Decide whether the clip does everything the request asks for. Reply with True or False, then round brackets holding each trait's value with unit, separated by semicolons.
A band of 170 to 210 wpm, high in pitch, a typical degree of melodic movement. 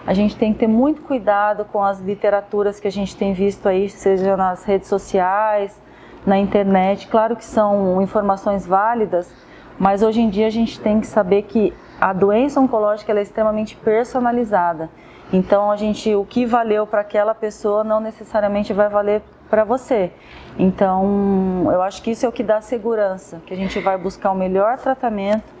False (180 wpm; 205 Hz; 1.9 semitones)